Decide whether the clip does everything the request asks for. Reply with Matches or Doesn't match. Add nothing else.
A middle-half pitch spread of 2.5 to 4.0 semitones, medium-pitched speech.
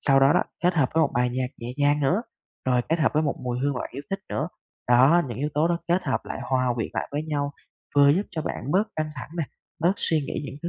Matches